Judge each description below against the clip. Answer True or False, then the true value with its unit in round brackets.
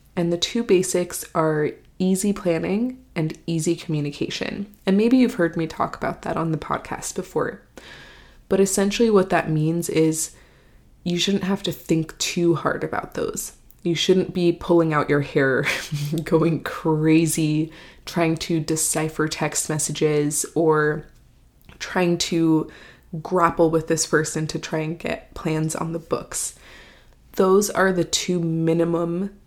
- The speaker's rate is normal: True (145 wpm)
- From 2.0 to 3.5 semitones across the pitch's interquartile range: True (2.5 semitones)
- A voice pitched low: False (165 Hz)